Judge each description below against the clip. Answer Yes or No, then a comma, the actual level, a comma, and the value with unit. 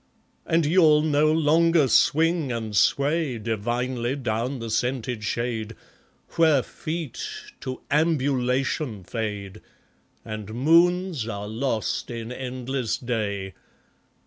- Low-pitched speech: Yes, low, 125 Hz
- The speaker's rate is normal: No, slow, 100 wpm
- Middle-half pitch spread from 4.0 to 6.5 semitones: Yes, average, 5.3 semitones